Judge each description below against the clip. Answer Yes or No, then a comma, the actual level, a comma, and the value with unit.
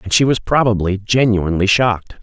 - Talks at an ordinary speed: Yes, average, 160 wpm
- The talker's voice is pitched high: No, low, 105 Hz